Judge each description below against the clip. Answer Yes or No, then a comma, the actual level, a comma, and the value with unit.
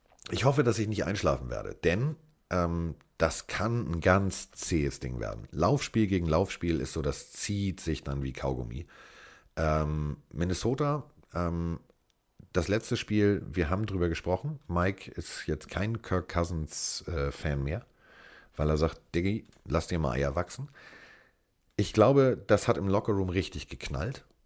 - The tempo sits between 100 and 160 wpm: Yes, average, 150 wpm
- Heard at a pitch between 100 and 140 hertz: No, very low, 90 Hz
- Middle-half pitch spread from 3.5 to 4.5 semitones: No, average, 5.2 semitones